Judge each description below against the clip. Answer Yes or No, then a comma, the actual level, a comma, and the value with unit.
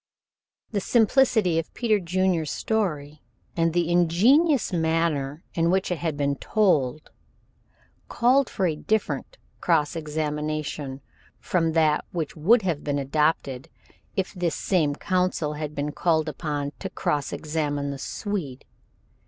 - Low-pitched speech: No, medium, 160 Hz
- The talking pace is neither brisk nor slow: No, slow, 130 wpm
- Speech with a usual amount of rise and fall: Yes, average, 3.9 semitones